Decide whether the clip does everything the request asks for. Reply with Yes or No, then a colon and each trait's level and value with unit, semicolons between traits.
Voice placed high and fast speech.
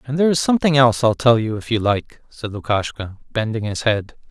No: low, 120 Hz; fast, 225 wpm